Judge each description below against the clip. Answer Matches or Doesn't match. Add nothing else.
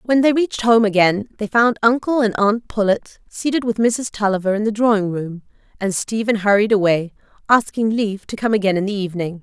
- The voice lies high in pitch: Matches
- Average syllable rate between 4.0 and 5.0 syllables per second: Doesn't match